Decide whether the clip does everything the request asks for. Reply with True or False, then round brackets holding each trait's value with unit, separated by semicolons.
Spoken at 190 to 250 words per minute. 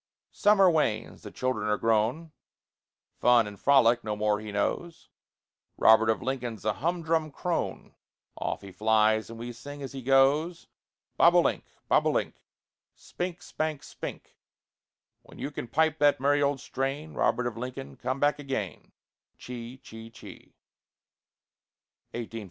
False (135 wpm)